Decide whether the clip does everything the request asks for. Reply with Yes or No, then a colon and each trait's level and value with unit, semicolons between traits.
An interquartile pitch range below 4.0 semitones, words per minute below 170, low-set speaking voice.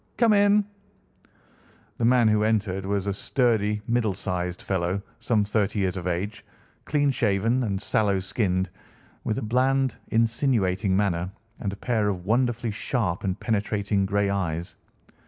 Yes: average, 3.4 semitones; average, 145 wpm; low, 105 Hz